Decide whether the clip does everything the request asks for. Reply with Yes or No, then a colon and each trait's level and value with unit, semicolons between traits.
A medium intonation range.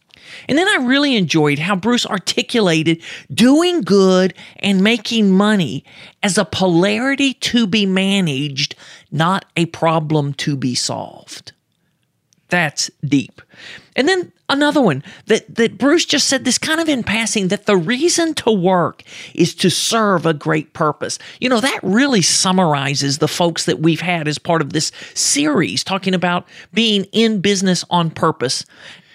No: wide, 6.0 semitones